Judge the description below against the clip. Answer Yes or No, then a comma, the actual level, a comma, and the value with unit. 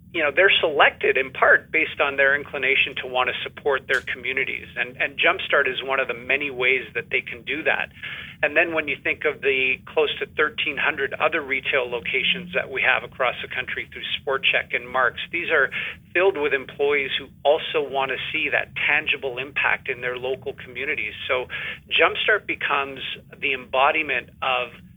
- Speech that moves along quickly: No, average, 185 wpm